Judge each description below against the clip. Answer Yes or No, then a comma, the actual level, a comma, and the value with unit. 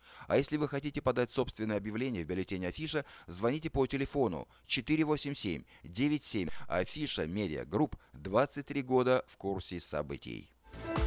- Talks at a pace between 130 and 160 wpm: No, average, 115 wpm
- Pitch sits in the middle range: No, low, 130 Hz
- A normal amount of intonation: No, wide, 6.5 semitones